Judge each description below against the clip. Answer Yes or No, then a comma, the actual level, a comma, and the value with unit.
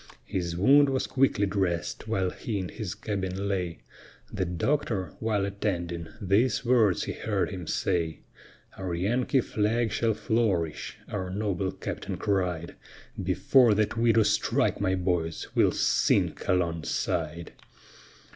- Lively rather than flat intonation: No, average, 3.8 semitones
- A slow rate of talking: Yes, slow, 130 wpm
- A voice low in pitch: Yes, low, 100 Hz